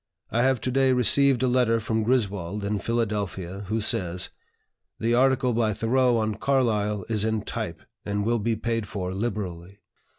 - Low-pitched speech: Yes, low, 110 Hz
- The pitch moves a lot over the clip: No, average, 3.0 semitones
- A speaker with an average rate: Yes, average, 165 wpm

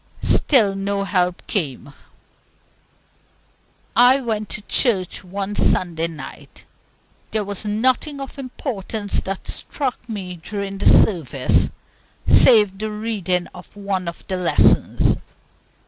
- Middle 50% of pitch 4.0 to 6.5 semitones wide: No, average, 3.3 semitones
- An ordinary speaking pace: No, slow, 115 wpm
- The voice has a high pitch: Yes, high, 200 Hz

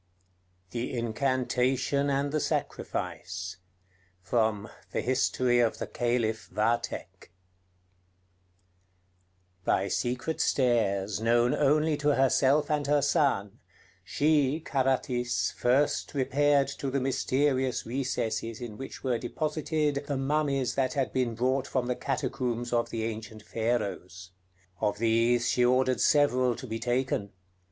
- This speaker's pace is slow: Yes, slow, 120 wpm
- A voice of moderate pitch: No, low, 125 Hz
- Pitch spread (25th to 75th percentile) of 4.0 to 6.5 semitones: No, average, 3.0 semitones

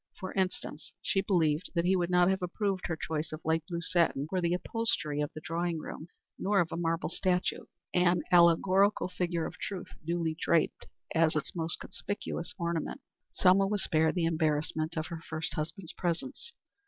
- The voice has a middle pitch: Yes, medium, 170 Hz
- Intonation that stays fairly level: Yes, narrow, 2.3 semitones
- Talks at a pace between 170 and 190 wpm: Yes, average, 180 wpm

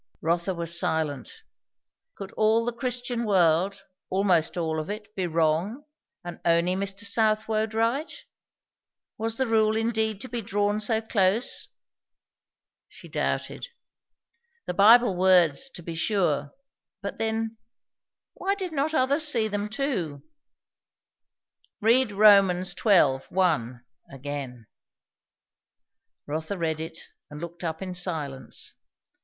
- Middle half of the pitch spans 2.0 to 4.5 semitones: No, average, 5.1 semitones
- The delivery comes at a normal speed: No, slow, 120 wpm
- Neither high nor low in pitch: No, high, 195 Hz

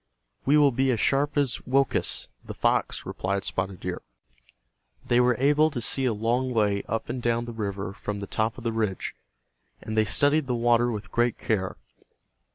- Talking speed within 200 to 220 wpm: No, average, 185 wpm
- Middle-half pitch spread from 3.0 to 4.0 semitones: Yes, average, 3.7 semitones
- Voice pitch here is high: No, low, 120 Hz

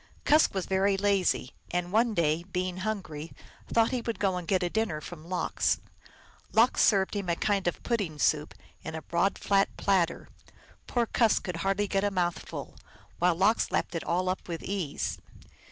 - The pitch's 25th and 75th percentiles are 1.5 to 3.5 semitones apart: Yes, average, 3.1 semitones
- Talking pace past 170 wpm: Yes, average, 180 wpm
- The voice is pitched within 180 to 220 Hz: Yes, medium, 185 Hz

